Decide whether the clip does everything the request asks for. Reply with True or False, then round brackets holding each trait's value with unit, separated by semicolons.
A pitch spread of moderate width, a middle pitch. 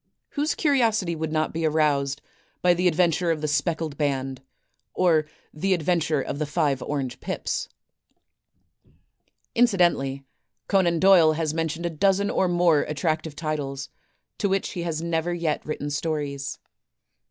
True (3.1 semitones; 160 Hz)